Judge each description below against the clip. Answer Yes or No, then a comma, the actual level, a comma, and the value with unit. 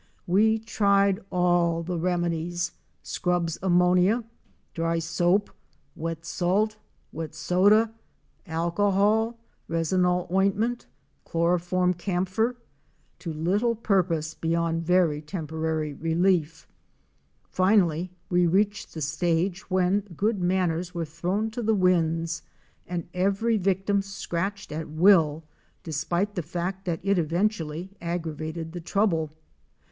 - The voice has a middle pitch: Yes, medium, 180 Hz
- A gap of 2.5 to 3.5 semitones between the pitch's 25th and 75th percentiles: Yes, average, 3.1 semitones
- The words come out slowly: Yes, slow, 110 wpm